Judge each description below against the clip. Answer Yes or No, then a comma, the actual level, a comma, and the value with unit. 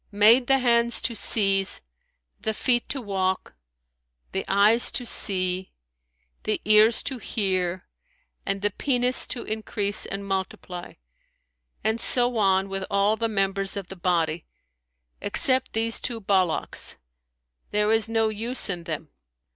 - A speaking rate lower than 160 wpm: Yes, slow, 135 wpm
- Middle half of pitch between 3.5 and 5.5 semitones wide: No, average, 3.1 semitones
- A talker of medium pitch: No, high, 205 Hz